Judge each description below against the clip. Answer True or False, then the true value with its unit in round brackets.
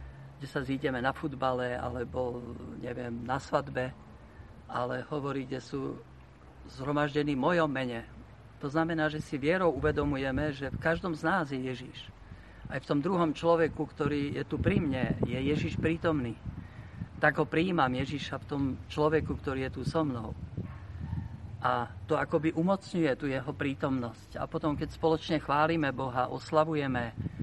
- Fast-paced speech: False (150 wpm)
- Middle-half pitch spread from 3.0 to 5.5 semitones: True (4.1 semitones)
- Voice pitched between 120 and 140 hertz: True (135 Hz)